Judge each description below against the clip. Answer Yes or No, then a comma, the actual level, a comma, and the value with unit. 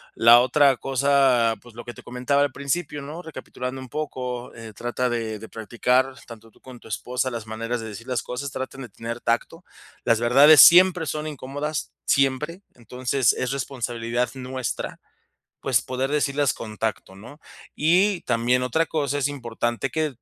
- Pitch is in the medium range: No, low, 130 Hz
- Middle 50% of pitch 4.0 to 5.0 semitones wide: No, average, 3.2 semitones